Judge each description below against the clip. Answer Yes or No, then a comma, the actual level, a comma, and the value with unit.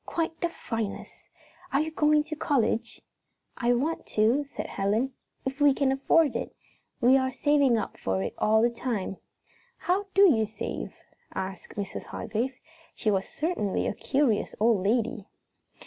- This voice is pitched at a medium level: No, very high, 250 Hz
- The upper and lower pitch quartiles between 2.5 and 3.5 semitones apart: No, average, 5.2 semitones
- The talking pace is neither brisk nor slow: Yes, average, 155 wpm